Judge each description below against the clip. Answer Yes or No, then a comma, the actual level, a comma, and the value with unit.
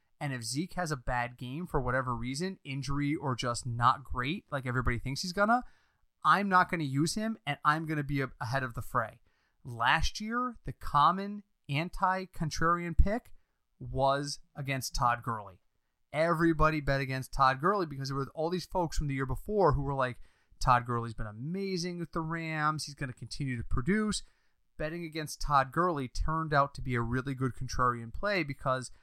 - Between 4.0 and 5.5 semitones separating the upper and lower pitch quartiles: Yes, average, 4.8 semitones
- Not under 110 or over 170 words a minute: No, average, 180 wpm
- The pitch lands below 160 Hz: Yes, medium, 140 Hz